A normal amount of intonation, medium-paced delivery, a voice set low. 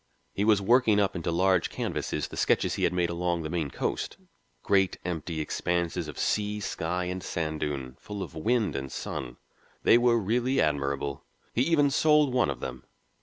No: wide, 5.7 semitones; average, 180 wpm; very low, 90 Hz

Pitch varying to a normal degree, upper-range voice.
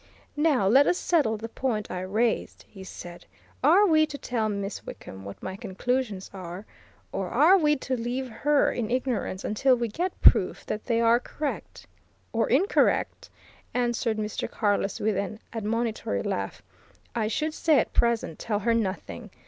Yes: average, 4.6 semitones; high, 230 Hz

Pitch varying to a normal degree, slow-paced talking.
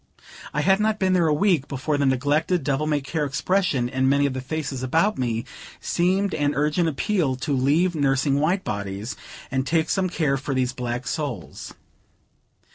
No: average, 4.3 semitones; average, 180 wpm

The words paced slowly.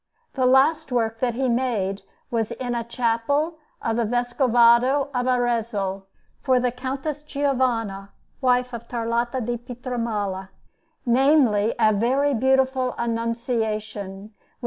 Yes: slow, 125 wpm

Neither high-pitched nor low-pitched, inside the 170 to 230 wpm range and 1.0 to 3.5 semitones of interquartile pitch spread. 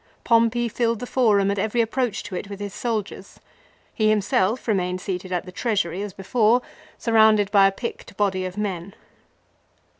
No: high, 205 Hz; average, 175 wpm; average, 2.9 semitones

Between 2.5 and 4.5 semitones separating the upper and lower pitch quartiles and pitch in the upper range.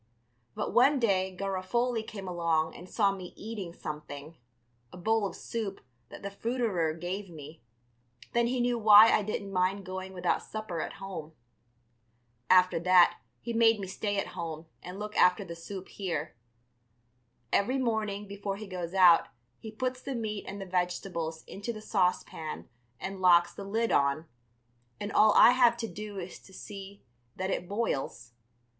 Yes: average, 3.3 semitones; high, 195 Hz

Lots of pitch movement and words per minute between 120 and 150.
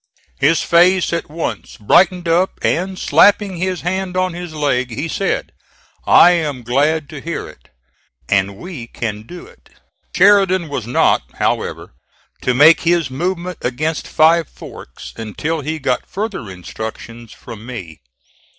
Yes: wide, 6.4 semitones; average, 140 wpm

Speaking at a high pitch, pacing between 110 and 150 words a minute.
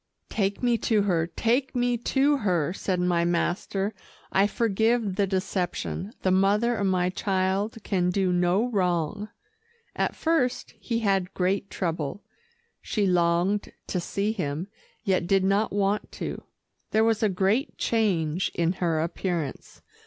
Yes: high, 195 Hz; average, 145 wpm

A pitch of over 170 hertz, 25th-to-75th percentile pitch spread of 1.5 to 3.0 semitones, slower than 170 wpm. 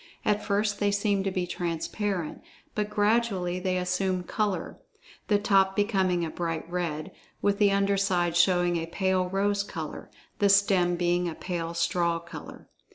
Yes: medium, 185 Hz; narrow, 2.5 semitones; average, 160 wpm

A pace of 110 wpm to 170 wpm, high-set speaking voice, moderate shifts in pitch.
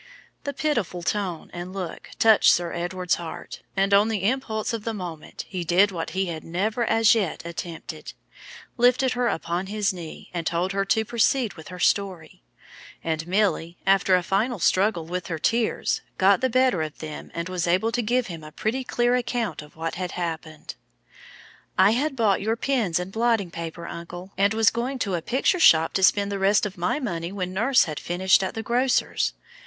No: average, 195 wpm; high, 195 Hz; average, 4.6 semitones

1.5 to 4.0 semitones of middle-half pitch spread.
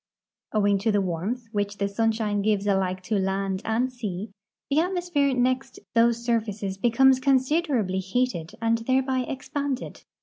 No: average, 4.4 semitones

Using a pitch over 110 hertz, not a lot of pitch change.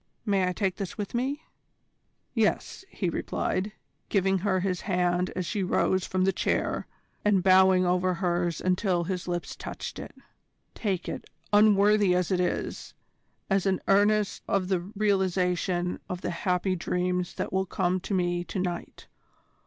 Yes: medium, 185 Hz; narrow, 1.7 semitones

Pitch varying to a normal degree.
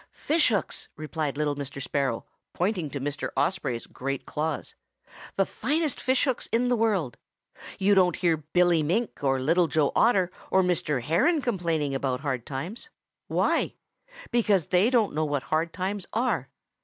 No: wide, 6.2 semitones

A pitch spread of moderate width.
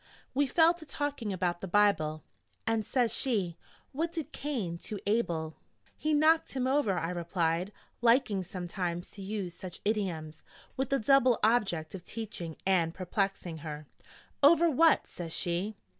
No: wide, 7.2 semitones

